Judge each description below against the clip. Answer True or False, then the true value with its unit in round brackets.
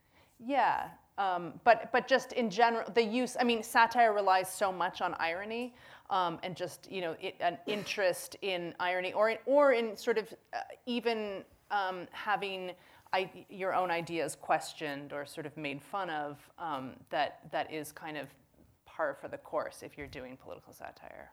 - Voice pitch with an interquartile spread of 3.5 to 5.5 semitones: True (4.8 semitones)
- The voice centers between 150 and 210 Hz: True (190 Hz)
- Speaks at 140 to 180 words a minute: True (175 wpm)